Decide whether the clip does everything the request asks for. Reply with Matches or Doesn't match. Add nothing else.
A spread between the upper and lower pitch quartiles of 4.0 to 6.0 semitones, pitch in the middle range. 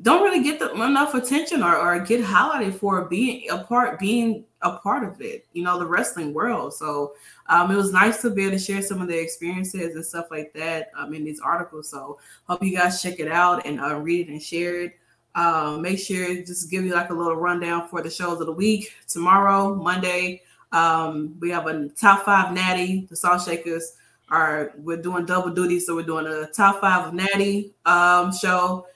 Doesn't match